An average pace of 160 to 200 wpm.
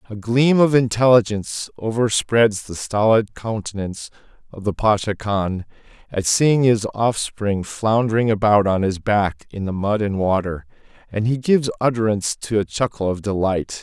No: average, 150 wpm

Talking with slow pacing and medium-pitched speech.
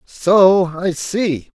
Yes: slow, 115 wpm; medium, 180 Hz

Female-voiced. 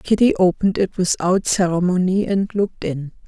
Yes: female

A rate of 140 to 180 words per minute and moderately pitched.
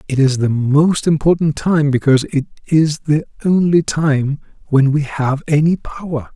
Yes: average, 160 wpm; medium, 150 Hz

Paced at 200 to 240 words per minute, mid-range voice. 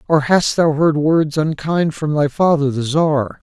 No: average, 190 wpm; medium, 150 Hz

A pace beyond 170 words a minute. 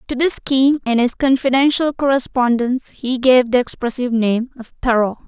No: average, 160 wpm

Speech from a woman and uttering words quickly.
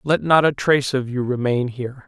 No: male; fast, 230 wpm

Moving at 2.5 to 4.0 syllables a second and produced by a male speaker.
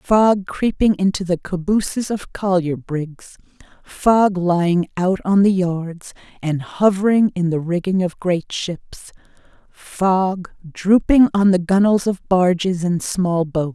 No: 3.7 syllables/s; female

